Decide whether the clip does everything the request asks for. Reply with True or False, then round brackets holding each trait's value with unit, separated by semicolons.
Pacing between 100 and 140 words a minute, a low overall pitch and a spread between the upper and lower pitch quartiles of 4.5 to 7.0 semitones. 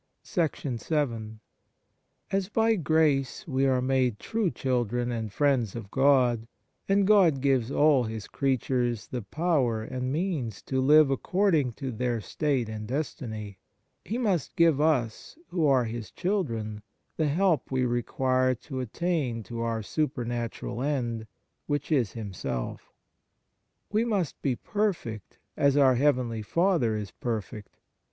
True (135 wpm; 130 Hz; 5.0 semitones)